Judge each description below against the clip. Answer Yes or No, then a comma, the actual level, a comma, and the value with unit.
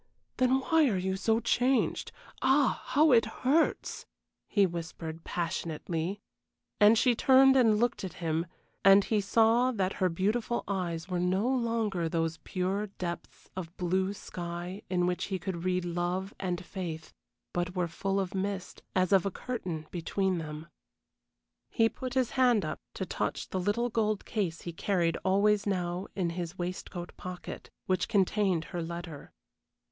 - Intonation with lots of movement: No, average, 3.9 semitones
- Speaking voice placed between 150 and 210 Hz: Yes, high, 190 Hz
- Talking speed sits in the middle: Yes, average, 155 wpm